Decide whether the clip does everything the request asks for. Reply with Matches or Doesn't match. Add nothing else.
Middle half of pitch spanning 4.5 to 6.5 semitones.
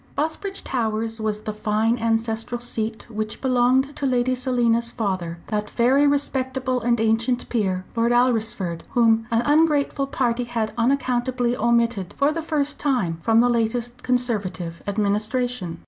Doesn't match